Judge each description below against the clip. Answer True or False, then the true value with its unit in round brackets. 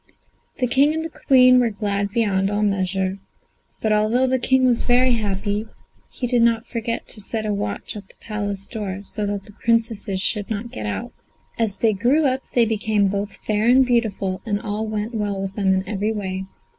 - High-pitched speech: True (215 Hz)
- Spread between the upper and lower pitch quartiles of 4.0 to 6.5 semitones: False (2.8 semitones)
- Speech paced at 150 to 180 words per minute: False (195 wpm)